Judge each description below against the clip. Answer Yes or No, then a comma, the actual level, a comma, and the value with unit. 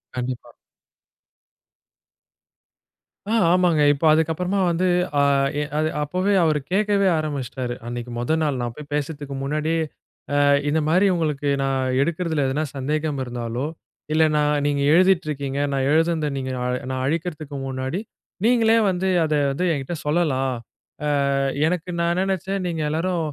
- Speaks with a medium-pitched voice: Yes, medium, 155 Hz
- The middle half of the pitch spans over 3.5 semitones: Yes, average, 4.1 semitones